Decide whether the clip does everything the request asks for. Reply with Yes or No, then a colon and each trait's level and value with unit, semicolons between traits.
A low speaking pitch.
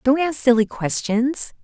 No: very high, 255 Hz